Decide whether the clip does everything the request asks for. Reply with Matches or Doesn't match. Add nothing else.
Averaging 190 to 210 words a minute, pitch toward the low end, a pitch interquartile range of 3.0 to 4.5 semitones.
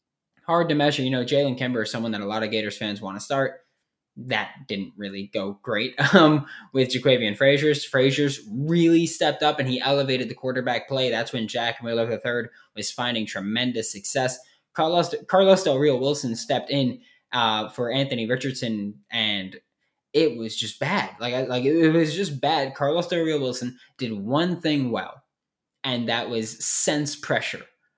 Doesn't match